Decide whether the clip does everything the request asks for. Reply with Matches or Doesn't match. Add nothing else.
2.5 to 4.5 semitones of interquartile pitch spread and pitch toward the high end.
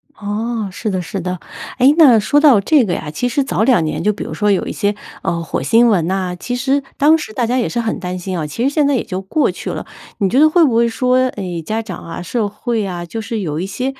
Doesn't match